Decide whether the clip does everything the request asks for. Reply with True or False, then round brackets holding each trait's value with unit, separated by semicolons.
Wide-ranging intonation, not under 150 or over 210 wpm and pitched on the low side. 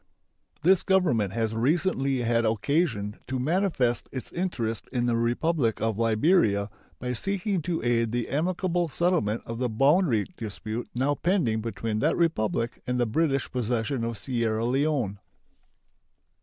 False (6.3 semitones; 140 wpm; 125 Hz)